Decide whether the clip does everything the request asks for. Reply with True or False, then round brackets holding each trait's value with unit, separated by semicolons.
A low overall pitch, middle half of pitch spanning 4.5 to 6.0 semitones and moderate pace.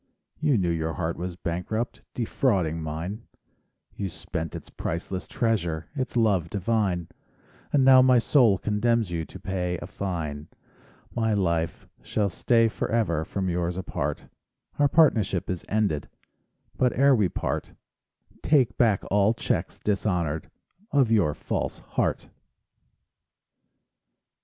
False (100 Hz; 5.2 semitones; 125 wpm)